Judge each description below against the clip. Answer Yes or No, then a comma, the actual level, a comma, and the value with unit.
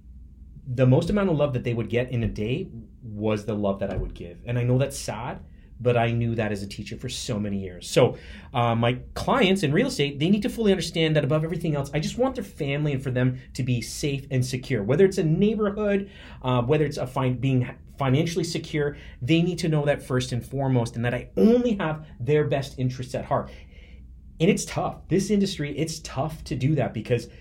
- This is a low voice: Yes, low, 130 Hz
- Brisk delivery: Yes, fast, 230 wpm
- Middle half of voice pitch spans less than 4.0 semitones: No, average, 5.2 semitones